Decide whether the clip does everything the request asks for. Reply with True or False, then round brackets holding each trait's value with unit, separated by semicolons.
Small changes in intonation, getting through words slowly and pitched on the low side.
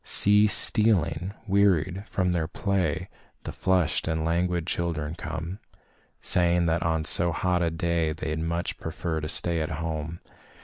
False (2.2 semitones; 145 wpm; 85 Hz)